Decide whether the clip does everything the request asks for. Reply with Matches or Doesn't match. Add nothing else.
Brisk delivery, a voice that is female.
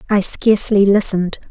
Doesn't match